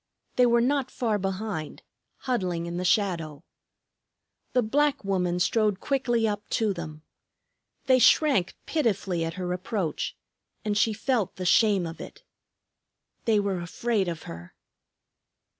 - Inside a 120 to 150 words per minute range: Yes, slow, 135 wpm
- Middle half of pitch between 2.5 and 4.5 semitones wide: No, average, 5.0 semitones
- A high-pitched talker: Yes, high, 200 Hz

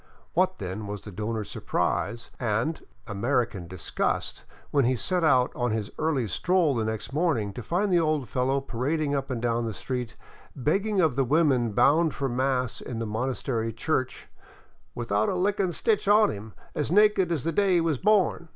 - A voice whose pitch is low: Yes, low, 130 Hz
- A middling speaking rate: Yes, average, 180 wpm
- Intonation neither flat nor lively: No, wide, 6.5 semitones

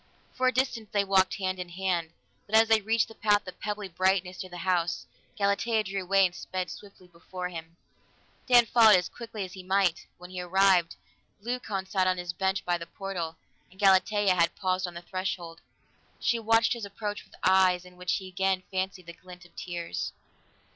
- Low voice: No, high, 190 Hz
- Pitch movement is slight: Yes, narrow, 2.3 semitones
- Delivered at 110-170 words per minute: No, average, 195 wpm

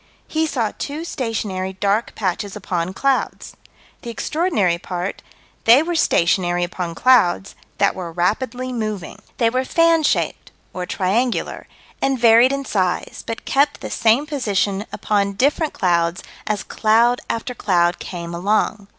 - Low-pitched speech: No, high, 215 Hz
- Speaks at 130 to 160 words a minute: Yes, average, 140 wpm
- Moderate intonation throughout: No, wide, 5.7 semitones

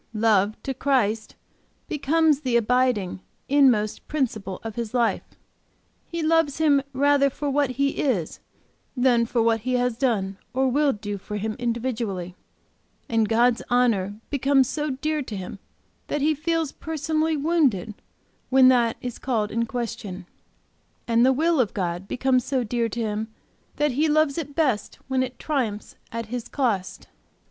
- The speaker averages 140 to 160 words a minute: Yes, average, 155 wpm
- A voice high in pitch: Yes, very high, 250 Hz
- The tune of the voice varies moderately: Yes, average, 4.4 semitones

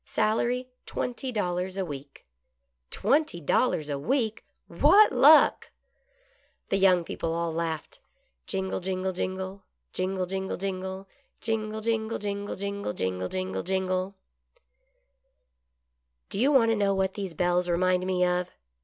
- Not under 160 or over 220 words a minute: No, average, 140 wpm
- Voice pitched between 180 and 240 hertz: Yes, high, 190 Hz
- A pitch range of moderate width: Yes, average, 4.2 semitones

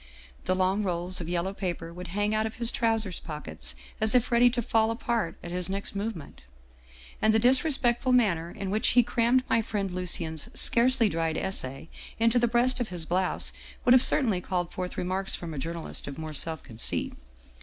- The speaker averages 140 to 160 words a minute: No, average, 195 wpm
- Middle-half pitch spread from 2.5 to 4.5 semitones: No, average, 5.2 semitones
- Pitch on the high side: Yes, high, 195 Hz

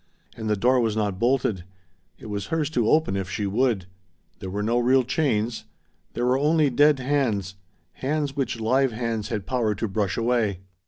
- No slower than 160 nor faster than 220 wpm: Yes, average, 180 wpm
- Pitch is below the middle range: Yes, low, 115 Hz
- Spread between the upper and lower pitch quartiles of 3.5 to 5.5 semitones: Yes, average, 4.1 semitones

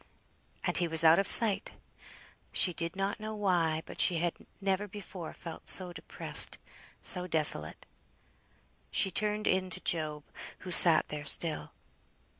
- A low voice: No, medium, 180 Hz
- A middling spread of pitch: Yes, average, 3.1 semitones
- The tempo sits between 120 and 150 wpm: Yes, average, 145 wpm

